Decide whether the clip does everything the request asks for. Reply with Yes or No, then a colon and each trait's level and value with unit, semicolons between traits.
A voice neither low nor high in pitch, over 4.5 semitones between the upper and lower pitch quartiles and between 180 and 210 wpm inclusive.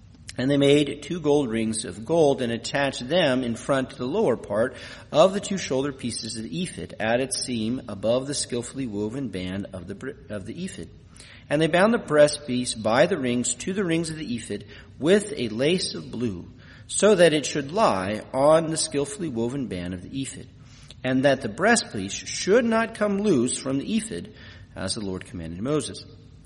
No: low, 130 Hz; wide, 5.5 semitones; average, 200 wpm